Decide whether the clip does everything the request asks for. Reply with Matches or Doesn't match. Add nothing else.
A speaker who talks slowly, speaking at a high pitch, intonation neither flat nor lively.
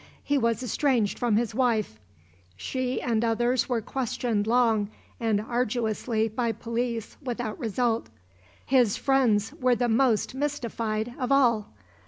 Doesn't match